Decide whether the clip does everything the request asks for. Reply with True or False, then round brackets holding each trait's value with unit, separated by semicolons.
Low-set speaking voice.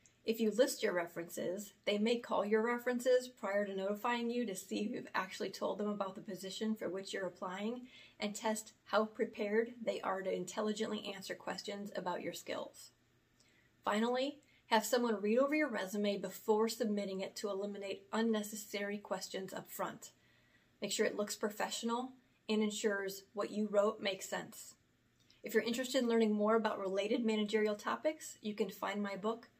False (215 Hz)